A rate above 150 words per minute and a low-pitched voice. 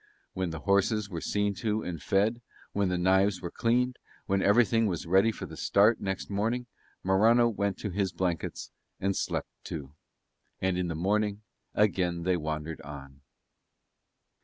Yes: average, 160 wpm; very low, 95 Hz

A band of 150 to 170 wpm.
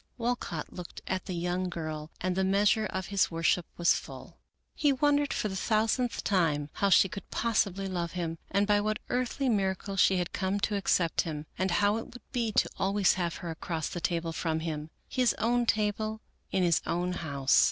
No: average, 195 wpm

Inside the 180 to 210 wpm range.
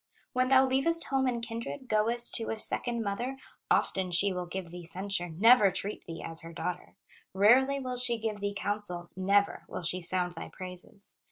Yes: average, 185 wpm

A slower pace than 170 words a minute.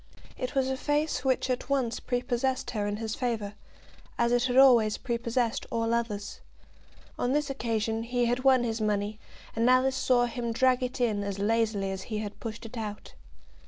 No: average, 185 wpm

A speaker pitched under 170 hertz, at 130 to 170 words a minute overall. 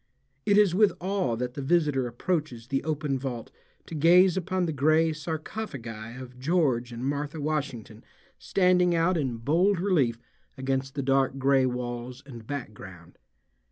Yes: medium, 140 Hz; average, 150 wpm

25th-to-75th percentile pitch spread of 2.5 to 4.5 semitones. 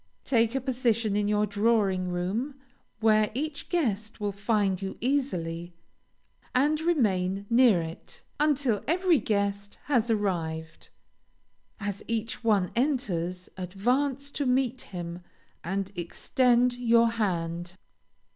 No: average, 5.1 semitones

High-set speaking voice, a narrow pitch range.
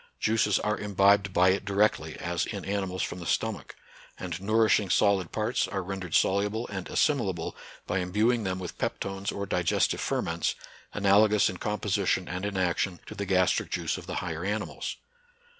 No: low, 100 Hz; narrow, 2.1 semitones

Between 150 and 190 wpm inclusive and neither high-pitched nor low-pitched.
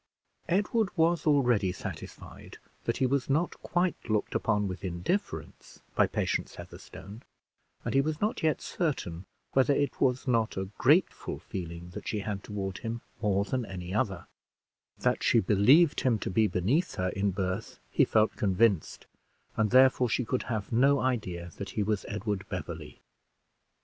No: average, 160 wpm; low, 110 Hz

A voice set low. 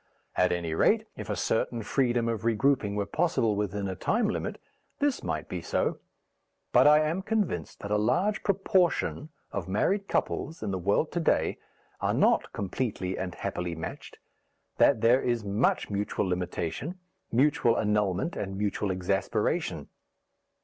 Yes: low, 110 Hz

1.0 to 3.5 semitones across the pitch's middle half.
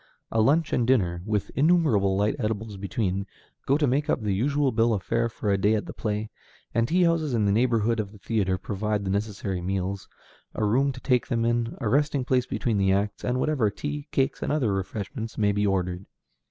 No: average, 4.3 semitones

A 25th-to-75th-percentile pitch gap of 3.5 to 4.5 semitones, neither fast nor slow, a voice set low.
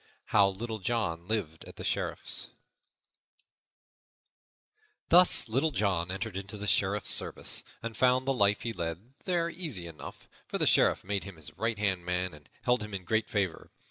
Yes: average, 4.1 semitones; average, 170 wpm; low, 105 Hz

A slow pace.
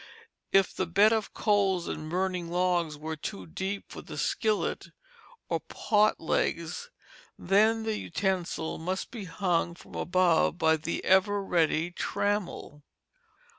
Yes: slow, 130 wpm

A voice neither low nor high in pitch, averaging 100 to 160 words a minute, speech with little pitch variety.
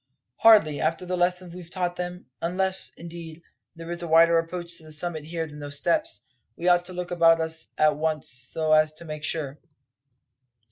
No: medium, 165 Hz; average, 190 wpm; narrow, 2.2 semitones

